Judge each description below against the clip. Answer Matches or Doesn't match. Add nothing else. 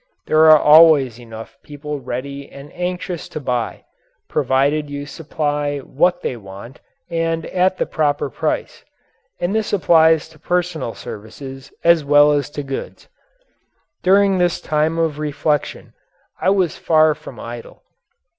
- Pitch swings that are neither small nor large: Matches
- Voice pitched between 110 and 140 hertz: Doesn't match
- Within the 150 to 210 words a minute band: Doesn't match